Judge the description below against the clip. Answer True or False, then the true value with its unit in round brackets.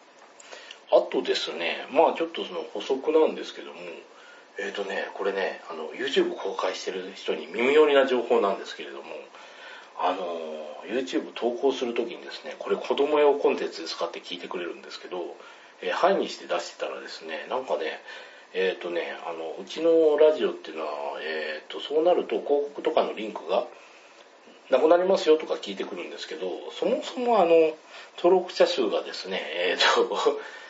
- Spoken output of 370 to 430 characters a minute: True (385 characters per minute)